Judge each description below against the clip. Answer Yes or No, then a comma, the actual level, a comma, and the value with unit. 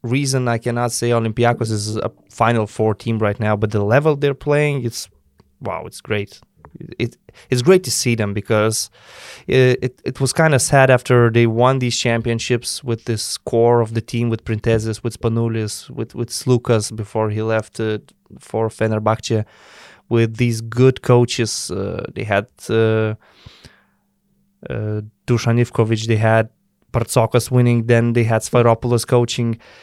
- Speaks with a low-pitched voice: Yes, low, 115 Hz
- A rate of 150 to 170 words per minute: Yes, average, 155 wpm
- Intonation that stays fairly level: Yes, narrow, 1.8 semitones